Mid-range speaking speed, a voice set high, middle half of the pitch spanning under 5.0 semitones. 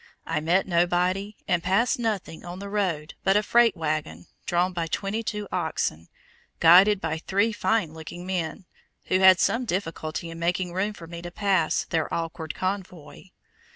No: average, 165 wpm; medium, 180 Hz; average, 3.3 semitones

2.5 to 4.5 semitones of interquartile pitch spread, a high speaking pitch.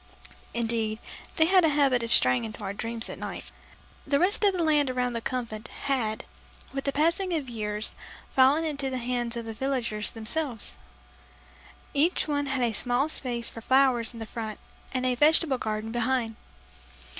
Yes: average, 3.8 semitones; very high, 250 Hz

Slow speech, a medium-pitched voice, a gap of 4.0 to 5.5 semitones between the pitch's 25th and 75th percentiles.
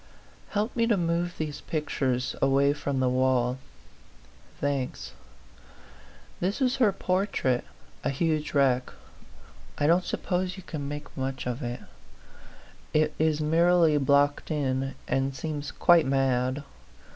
Yes: slow, 125 wpm; medium, 145 Hz; average, 4.3 semitones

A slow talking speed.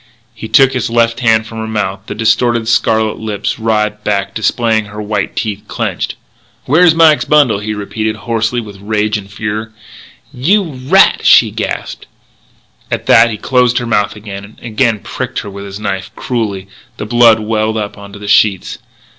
No: average, 175 wpm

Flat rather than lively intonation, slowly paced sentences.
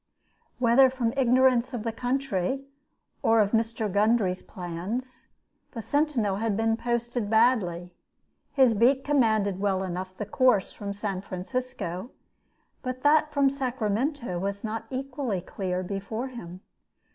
No: average, 4.5 semitones; slow, 130 wpm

